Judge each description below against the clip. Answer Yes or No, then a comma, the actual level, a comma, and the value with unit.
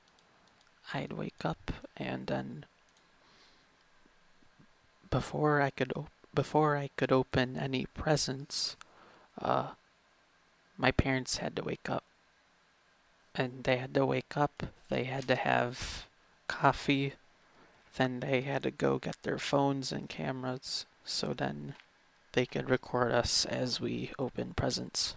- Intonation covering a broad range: Yes, wide, 6.6 semitones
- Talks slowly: Yes, slow, 125 wpm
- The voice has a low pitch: Yes, low, 130 Hz